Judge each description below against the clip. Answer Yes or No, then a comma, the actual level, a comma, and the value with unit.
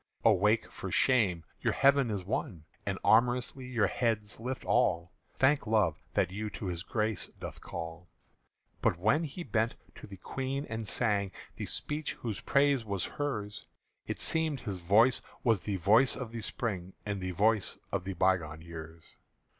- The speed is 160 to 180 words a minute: Yes, average, 165 wpm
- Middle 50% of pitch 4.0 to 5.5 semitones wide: Yes, average, 5.1 semitones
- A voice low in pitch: Yes, low, 105 Hz